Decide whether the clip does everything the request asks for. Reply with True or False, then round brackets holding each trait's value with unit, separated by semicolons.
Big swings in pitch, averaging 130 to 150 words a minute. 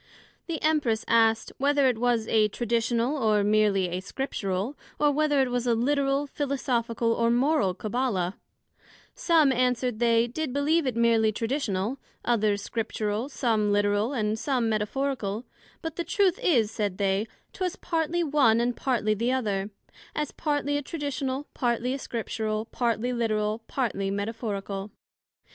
False (4.4 semitones; 145 wpm)